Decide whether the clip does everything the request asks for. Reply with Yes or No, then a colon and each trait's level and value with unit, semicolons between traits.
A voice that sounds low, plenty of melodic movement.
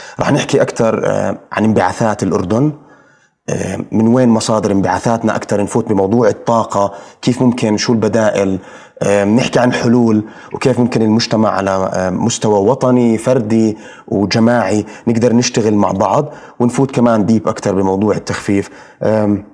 No: low, 110 Hz; average, 2.7 semitones